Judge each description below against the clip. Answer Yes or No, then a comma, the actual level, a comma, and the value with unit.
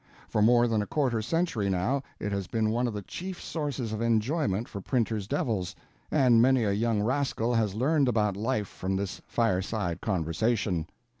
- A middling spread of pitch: Yes, average, 3.8 semitones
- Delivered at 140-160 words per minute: No, average, 175 wpm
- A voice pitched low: Yes, low, 110 Hz